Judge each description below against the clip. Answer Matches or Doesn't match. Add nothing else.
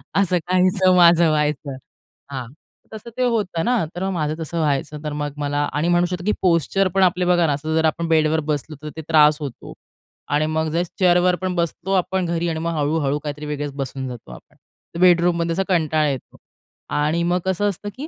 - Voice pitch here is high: Doesn't match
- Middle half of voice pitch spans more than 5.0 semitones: Doesn't match